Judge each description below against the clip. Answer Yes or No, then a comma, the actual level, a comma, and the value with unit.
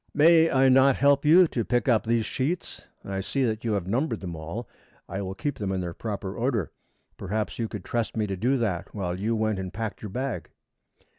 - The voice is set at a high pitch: No, low, 110 Hz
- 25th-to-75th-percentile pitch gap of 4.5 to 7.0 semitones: Yes, average, 5.1 semitones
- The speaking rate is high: Yes, fast, 220 wpm